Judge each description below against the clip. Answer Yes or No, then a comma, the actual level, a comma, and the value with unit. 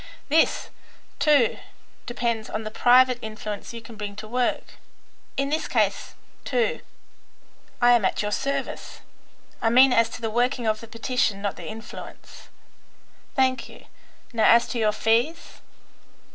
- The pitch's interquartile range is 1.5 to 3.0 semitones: Yes, narrow, 2.6 semitones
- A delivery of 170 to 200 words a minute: No, average, 145 wpm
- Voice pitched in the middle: No, high, 235 Hz